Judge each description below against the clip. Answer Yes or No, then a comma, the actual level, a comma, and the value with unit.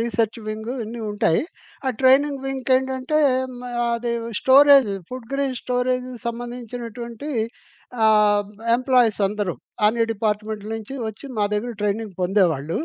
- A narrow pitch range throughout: No, average, 3.3 semitones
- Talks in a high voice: Yes, high, 235 Hz